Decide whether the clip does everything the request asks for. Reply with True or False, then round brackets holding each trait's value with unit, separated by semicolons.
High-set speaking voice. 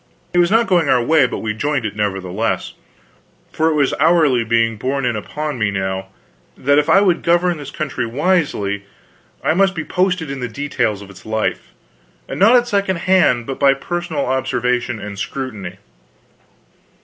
False (140 Hz)